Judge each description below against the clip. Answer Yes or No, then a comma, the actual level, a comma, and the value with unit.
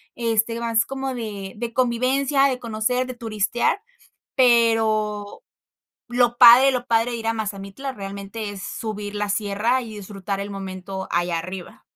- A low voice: No, high, 225 Hz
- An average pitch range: Yes, average, 3.2 semitones